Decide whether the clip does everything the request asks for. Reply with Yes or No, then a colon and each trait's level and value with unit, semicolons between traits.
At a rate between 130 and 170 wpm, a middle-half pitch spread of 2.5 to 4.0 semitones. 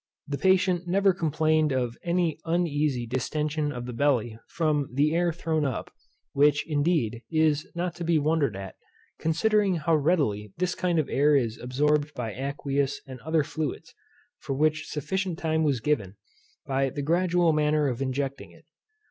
Yes: average, 160 wpm; average, 3.3 semitones